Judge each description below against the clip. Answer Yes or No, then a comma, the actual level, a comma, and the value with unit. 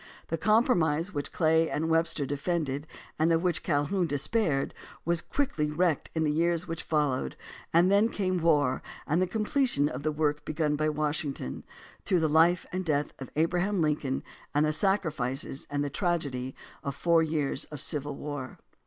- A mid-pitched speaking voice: Yes, medium, 155 Hz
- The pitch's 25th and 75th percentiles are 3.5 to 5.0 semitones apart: No, average, 3.0 semitones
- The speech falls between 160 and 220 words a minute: Yes, average, 170 wpm